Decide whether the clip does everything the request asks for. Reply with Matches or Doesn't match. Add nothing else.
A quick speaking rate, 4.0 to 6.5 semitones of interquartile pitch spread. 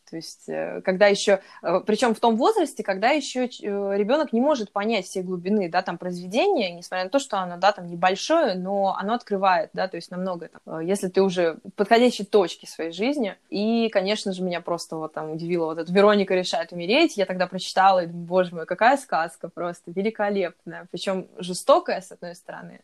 Doesn't match